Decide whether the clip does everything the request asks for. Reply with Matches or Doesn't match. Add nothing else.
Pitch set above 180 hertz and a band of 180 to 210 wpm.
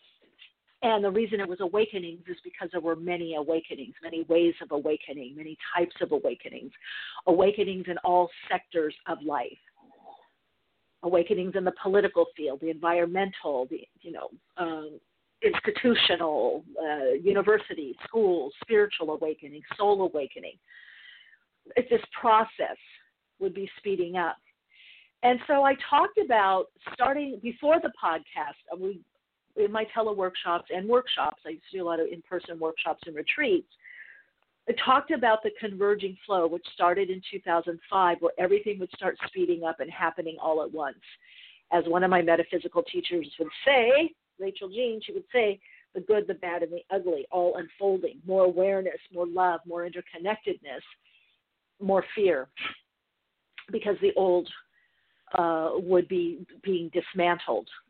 Doesn't match